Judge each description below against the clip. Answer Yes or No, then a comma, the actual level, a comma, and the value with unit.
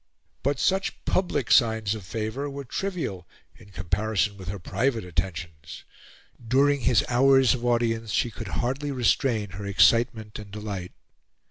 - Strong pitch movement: No, average, 4.8 semitones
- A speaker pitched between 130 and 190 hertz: No, low, 110 Hz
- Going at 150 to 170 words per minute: No, average, 140 wpm